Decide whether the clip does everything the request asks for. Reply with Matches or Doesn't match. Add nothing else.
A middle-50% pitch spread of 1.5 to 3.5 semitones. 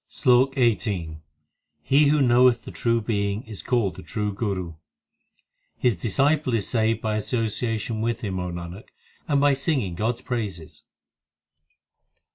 Doesn't match